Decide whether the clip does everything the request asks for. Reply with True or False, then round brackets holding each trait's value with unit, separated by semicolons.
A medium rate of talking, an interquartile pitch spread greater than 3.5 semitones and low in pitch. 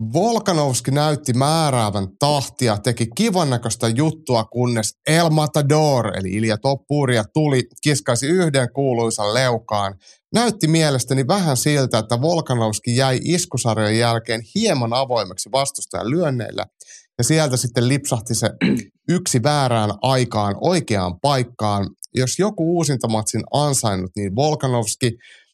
True (115 wpm; 4.8 semitones; 130 Hz)